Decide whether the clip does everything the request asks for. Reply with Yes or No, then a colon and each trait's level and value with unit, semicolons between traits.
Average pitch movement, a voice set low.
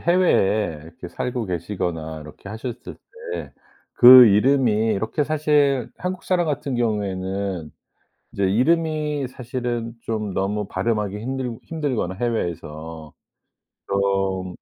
No: wide, 5.8 semitones; low, 110 Hz